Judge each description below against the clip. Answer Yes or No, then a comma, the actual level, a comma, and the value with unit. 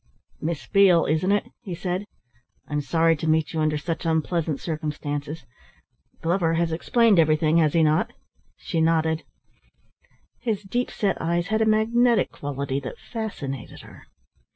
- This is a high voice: No, medium, 165 Hz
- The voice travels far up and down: No, average, 4.1 semitones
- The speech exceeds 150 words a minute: No, average, 145 wpm